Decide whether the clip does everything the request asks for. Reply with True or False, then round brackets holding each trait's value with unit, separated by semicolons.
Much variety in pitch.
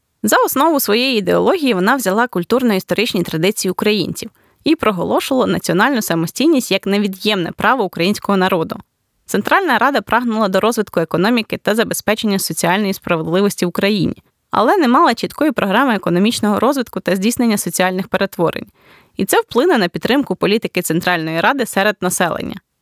False (4.8 semitones)